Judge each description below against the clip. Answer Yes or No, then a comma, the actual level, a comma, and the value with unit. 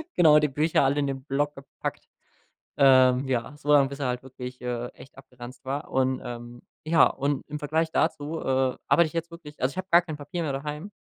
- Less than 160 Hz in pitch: Yes, medium, 140 Hz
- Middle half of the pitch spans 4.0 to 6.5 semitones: No, narrow, 2.6 semitones